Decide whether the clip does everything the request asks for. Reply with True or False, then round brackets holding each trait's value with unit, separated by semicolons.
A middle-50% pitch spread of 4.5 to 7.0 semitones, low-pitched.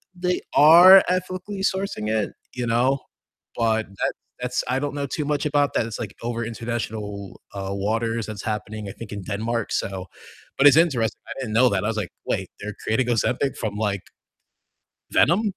True (5.2 semitones; 115 Hz)